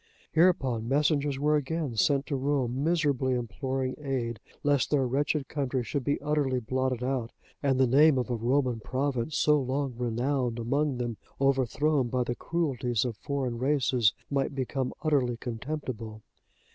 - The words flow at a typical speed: Yes, average, 150 wpm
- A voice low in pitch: Yes, low, 130 Hz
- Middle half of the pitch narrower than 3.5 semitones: Yes, average, 2.8 semitones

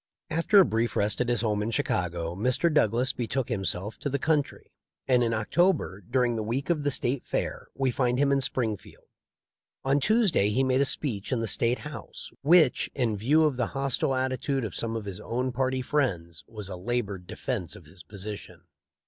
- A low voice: Yes, low, 120 Hz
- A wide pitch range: No, average, 4.5 semitones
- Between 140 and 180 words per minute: No, average, 200 wpm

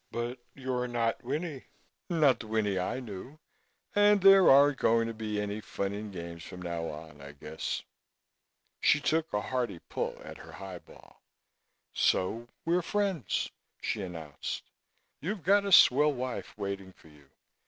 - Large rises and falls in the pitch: Yes, wide, 7.7 semitones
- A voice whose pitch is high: No, low, 115 Hz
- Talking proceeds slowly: No, average, 155 wpm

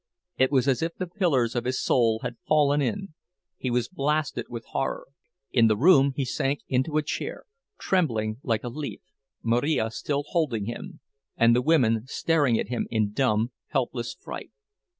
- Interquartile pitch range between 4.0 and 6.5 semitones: Yes, average, 4.6 semitones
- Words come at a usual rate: Yes, average, 170 wpm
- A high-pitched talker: No, low, 130 Hz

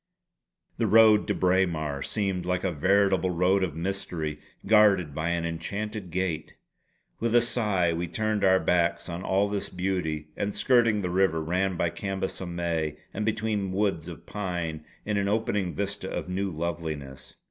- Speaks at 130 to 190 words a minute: Yes, average, 165 wpm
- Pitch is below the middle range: Yes, very low, 95 Hz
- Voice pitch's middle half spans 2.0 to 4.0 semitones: Yes, average, 3.1 semitones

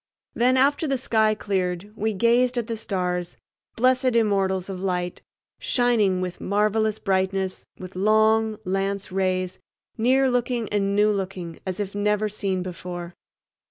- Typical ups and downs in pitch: Yes, average, 3.0 semitones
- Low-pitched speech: No, high, 205 Hz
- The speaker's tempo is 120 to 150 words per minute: Yes, average, 140 wpm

